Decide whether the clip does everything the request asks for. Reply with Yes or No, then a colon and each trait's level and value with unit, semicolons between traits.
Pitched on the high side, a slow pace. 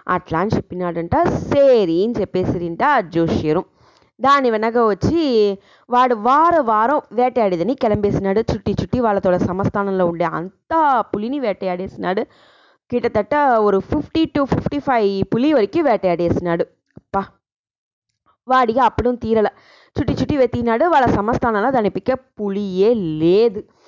Yes: high, 220 Hz; slow, 105 wpm